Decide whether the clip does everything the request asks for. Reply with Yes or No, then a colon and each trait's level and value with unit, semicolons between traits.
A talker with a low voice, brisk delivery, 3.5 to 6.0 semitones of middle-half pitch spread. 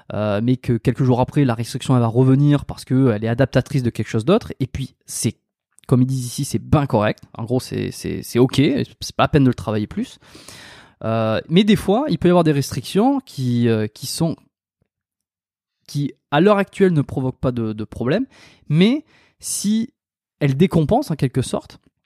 No: low, 130 Hz; average, 200 wpm; average, 4.5 semitones